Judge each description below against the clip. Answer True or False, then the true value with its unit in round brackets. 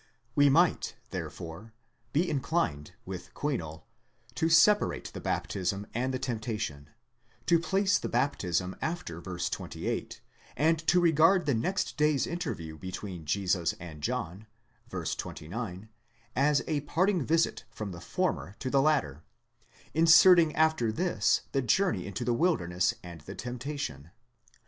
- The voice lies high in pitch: False (125 Hz)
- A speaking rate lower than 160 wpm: True (135 wpm)